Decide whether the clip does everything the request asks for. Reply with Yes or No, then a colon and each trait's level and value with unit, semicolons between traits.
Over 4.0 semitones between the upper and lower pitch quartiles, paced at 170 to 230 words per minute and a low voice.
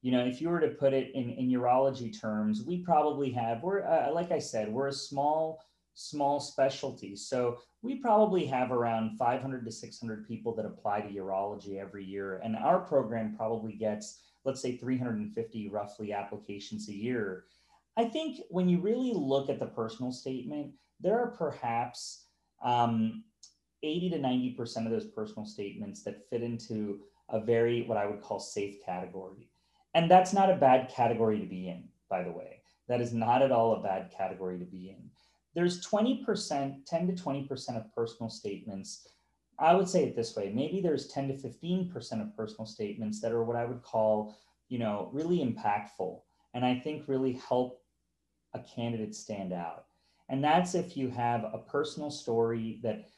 Yes: average, 4.6 semitones; average, 180 wpm; low, 120 Hz